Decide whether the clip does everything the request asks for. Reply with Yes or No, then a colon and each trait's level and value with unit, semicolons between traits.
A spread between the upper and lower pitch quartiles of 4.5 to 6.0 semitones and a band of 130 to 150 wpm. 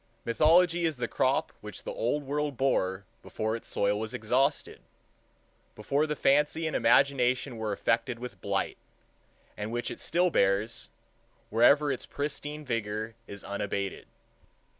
Yes: average, 5.3 semitones; average, 140 wpm